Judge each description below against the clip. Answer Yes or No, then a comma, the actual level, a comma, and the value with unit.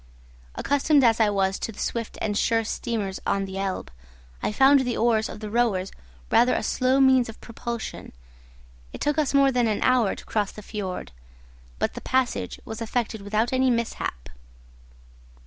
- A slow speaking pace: No, average, 175 wpm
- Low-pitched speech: No, high, 230 Hz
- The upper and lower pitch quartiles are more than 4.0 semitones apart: No, average, 3.6 semitones